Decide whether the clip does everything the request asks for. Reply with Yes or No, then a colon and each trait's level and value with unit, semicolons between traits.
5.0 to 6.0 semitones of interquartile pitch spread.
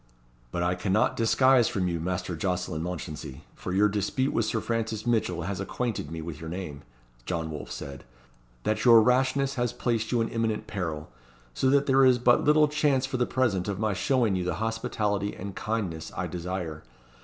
Yes: average, 5.3 semitones